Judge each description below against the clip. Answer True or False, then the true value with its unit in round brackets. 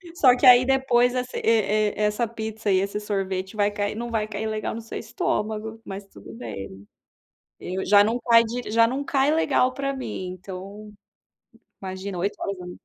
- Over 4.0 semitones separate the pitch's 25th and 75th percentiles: False (3.3 semitones)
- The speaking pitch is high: True (215 Hz)